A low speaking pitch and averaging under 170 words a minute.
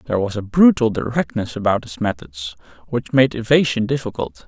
Yes: low, 120 Hz; average, 160 wpm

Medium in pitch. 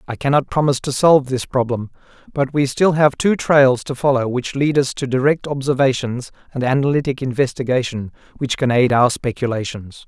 No: low, 130 Hz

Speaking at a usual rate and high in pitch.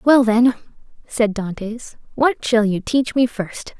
Yes: average, 160 wpm; high, 230 Hz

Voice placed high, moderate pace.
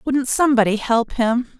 Yes: high, 245 Hz; average, 150 wpm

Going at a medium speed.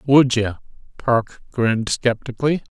No: slow, 110 wpm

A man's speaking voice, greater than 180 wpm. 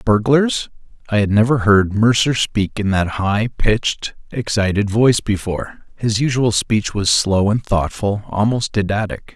No: male; average, 145 wpm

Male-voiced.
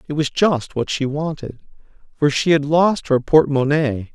Yes: male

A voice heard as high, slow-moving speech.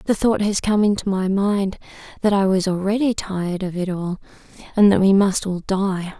No: high, 195 Hz; fast, 205 wpm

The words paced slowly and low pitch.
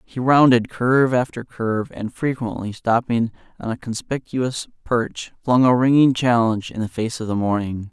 No: average, 165 wpm; low, 120 Hz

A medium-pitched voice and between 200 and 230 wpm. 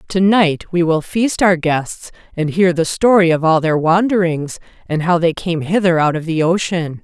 Yes: medium, 170 Hz; fast, 205 wpm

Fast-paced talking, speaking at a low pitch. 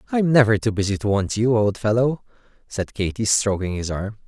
No: average, 195 wpm; low, 110 Hz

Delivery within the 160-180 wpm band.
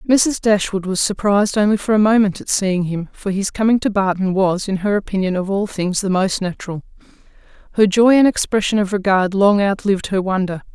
No: average, 200 wpm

